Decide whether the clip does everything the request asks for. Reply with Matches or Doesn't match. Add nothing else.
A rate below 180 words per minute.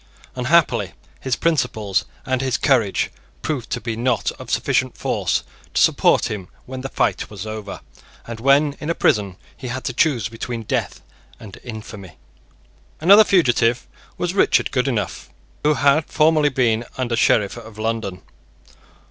Matches